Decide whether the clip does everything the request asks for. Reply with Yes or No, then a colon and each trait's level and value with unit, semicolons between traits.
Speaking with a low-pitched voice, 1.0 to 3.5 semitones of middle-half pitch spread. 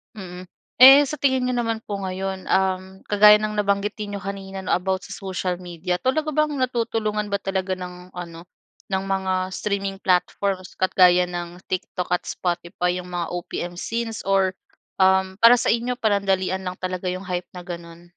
No: high, 190 Hz; narrow, 2.6 semitones